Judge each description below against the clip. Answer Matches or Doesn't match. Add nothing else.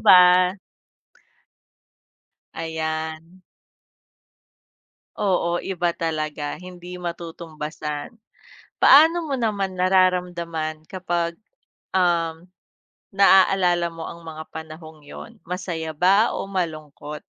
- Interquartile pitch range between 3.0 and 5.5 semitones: Doesn't match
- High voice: Doesn't match